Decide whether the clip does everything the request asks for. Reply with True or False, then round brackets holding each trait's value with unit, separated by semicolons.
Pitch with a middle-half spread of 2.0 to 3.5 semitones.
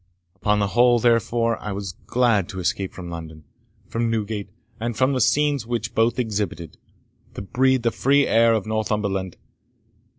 True (3.1 semitones)